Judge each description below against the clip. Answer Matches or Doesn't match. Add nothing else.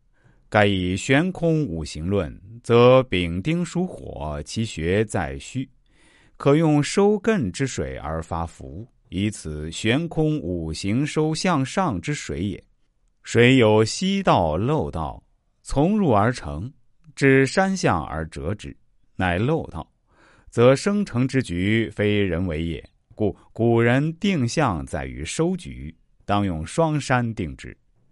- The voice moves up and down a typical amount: Doesn't match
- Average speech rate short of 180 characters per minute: Matches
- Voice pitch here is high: Doesn't match